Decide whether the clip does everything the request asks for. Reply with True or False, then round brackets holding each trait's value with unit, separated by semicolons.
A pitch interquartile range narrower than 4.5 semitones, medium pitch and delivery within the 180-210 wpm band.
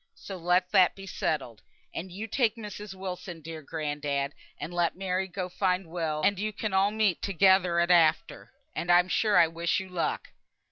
True (2.7 semitones; 180 Hz; 185 wpm)